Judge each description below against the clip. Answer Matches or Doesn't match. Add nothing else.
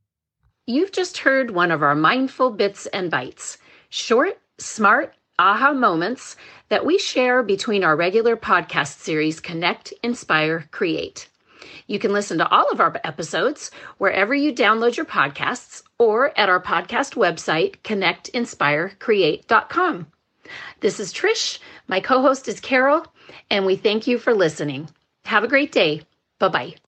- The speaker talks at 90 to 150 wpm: Matches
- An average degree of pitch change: Doesn't match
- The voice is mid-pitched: Doesn't match